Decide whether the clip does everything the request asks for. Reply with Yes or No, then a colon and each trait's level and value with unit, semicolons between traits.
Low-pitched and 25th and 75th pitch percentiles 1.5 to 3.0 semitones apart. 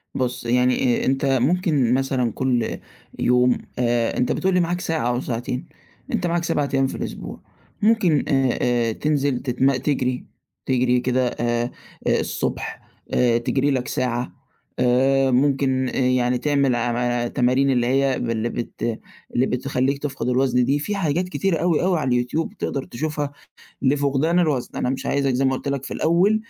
Yes: low, 130 Hz; average, 2.7 semitones